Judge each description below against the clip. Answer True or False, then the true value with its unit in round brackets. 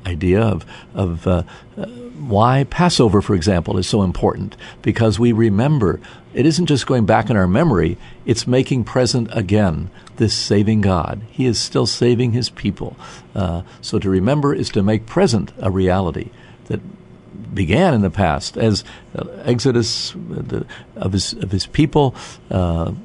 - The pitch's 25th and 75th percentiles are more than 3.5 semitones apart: True (4.5 semitones)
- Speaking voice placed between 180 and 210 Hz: False (110 Hz)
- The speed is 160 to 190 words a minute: True (165 wpm)